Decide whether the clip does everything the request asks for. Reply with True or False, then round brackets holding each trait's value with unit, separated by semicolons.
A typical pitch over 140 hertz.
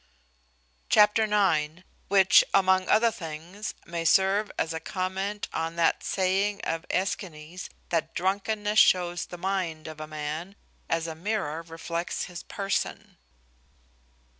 True (185 Hz)